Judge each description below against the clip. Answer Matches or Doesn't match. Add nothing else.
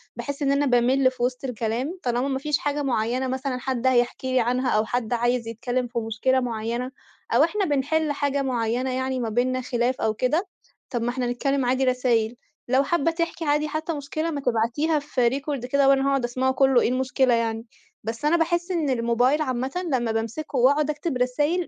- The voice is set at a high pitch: Matches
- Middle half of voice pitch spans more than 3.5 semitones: Doesn't match